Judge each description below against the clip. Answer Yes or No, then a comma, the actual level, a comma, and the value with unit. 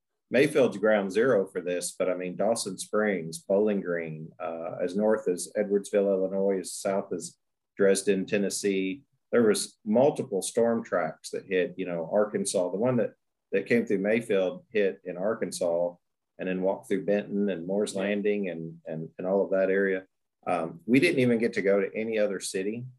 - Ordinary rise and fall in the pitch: No, narrow, 2.3 semitones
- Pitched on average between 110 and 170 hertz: No, low, 100 Hz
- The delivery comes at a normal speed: Yes, average, 180 wpm